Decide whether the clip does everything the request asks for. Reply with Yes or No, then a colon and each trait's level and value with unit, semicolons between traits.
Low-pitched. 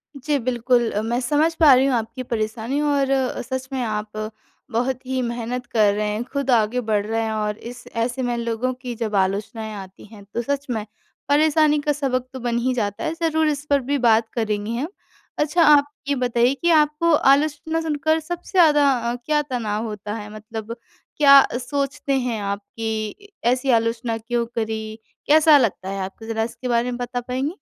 No: high, 245 Hz